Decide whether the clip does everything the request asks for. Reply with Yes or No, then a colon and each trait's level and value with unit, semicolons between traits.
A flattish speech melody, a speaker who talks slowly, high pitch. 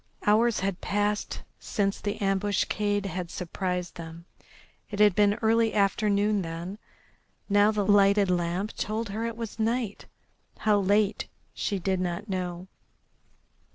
Yes: narrow, 2.2 semitones; slow, 130 wpm; high, 205 Hz